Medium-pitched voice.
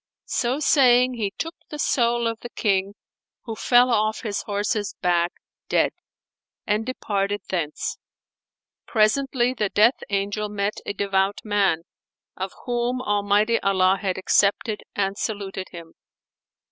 No: high, 210 Hz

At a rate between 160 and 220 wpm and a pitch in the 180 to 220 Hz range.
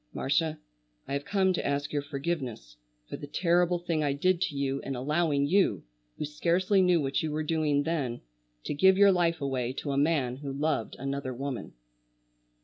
No: average, 185 wpm; medium, 150 Hz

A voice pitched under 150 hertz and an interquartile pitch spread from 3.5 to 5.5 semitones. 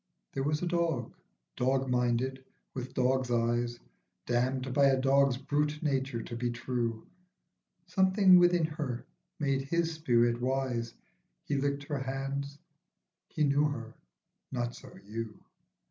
No: low, 135 Hz; average, 3.1 semitones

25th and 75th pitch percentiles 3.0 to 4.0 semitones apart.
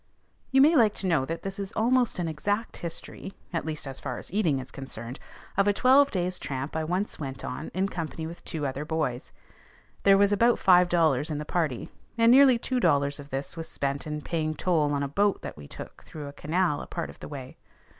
No: wide, 5.6 semitones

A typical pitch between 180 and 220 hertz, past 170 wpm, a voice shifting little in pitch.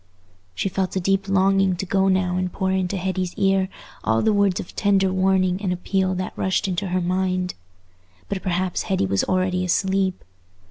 Yes: medium, 185 Hz; average, 180 wpm; narrow, 1.0 semitones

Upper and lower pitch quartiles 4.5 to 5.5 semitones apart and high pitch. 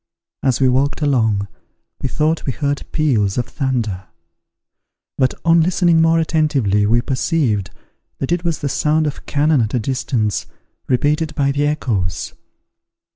No: average, 4.8 semitones; medium, 140 Hz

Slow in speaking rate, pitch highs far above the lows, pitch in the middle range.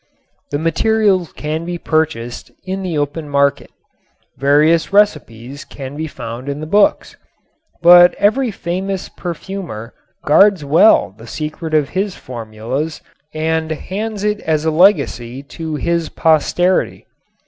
No: slow, 125 wpm; average, 4.6 semitones; medium, 160 Hz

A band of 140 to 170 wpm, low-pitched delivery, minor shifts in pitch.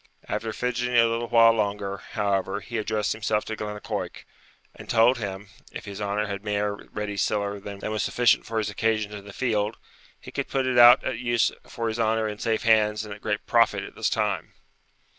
No: average, 200 wpm; low, 110 Hz; narrow, 1.9 semitones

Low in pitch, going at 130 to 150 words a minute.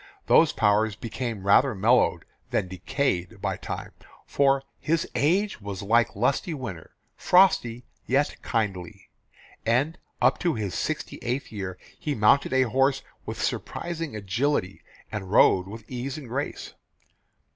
Yes: low, 120 Hz; slow, 135 wpm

